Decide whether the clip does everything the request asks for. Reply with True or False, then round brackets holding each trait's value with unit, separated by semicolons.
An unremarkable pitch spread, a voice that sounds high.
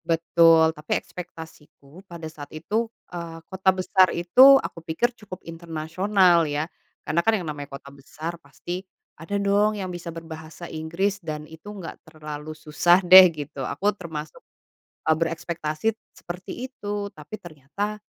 False (3.3 semitones; 170 Hz)